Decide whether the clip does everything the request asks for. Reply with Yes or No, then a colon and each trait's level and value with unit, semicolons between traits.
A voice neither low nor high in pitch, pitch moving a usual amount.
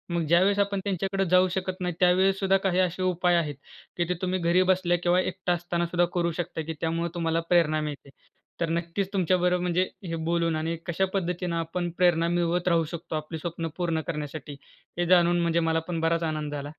No: medium, 175 Hz; narrow, 1.6 semitones